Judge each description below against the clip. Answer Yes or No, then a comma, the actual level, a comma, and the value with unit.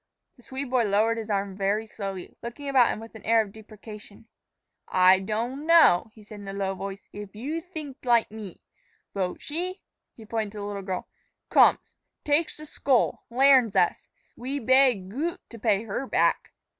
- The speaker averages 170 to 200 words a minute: Yes, average, 180 wpm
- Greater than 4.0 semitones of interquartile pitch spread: Yes, average, 4.7 semitones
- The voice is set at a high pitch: Yes, high, 220 Hz